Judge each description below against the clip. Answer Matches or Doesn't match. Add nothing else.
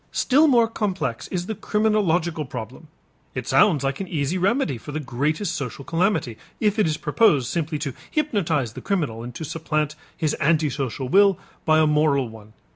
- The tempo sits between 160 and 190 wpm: Matches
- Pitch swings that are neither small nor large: Doesn't match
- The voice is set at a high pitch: Doesn't match